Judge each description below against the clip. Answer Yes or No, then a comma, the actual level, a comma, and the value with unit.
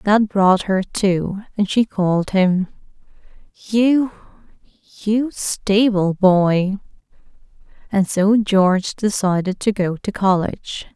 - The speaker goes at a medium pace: No, slow, 100 wpm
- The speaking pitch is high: Yes, high, 200 Hz